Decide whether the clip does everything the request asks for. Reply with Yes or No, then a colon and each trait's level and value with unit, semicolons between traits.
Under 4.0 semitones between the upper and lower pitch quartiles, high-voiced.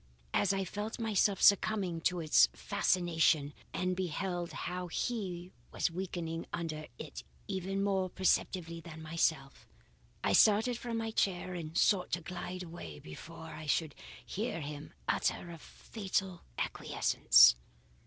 No: average, 3.1 semitones; medium, 180 Hz